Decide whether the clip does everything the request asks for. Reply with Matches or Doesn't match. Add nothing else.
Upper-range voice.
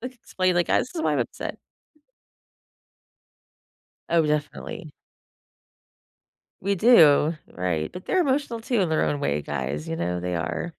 Doesn't match